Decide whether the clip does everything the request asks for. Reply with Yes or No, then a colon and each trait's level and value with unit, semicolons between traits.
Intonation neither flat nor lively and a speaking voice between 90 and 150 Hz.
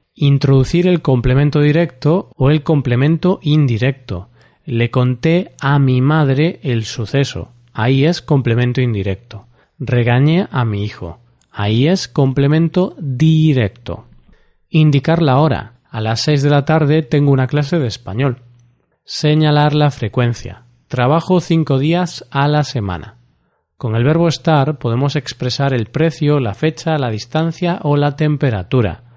Yes: average, 4.4 semitones; medium, 140 Hz